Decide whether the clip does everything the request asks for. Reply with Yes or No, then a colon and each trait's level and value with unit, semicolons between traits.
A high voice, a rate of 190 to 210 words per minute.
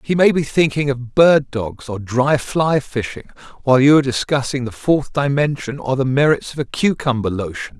No: low, 135 Hz; average, 195 wpm